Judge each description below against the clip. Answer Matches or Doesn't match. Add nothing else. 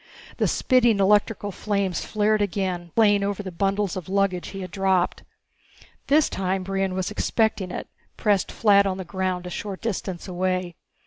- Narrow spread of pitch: Matches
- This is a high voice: Matches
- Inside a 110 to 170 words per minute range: Matches